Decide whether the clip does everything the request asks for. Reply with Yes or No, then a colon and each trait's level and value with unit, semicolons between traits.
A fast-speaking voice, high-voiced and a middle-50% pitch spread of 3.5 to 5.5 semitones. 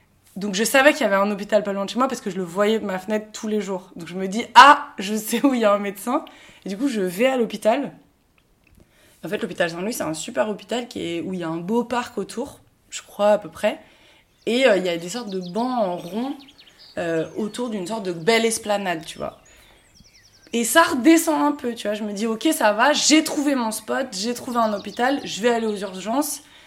Yes: fast, 255 wpm; high, 220 Hz; average, 4.1 semitones